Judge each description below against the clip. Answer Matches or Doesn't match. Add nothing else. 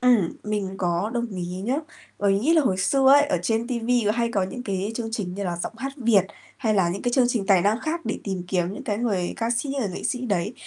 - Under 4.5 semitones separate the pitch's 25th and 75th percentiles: Matches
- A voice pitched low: Doesn't match